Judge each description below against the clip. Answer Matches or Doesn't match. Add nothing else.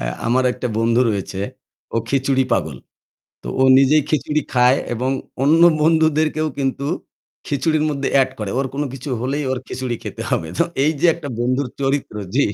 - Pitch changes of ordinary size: Matches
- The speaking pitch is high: Doesn't match